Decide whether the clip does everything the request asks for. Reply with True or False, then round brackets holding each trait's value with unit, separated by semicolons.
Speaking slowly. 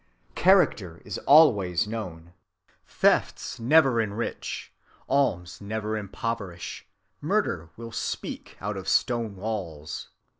True (100 wpm)